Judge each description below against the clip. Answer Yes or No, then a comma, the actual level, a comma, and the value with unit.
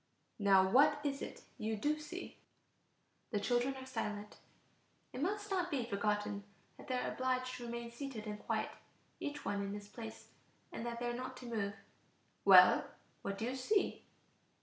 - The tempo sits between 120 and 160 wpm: No, average, 170 wpm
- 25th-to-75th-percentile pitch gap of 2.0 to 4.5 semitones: Yes, average, 4.1 semitones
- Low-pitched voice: No, high, 240 Hz